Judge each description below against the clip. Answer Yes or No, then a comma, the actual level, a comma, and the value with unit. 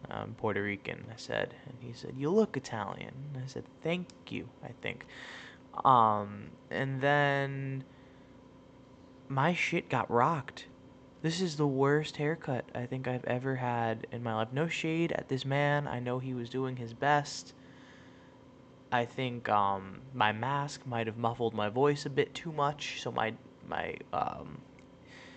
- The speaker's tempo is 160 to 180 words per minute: Yes, average, 165 wpm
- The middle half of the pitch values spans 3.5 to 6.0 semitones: No, average, 3.1 semitones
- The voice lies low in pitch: Yes, low, 130 Hz